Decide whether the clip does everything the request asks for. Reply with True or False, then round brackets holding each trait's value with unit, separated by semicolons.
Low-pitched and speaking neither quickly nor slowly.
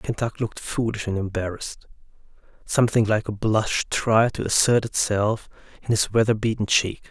True (110 Hz; 150 wpm)